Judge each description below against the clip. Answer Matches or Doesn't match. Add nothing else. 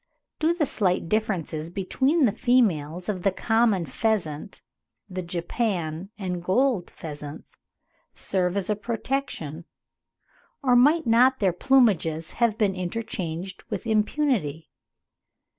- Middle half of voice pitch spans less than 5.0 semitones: Doesn't match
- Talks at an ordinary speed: Doesn't match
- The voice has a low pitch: Doesn't match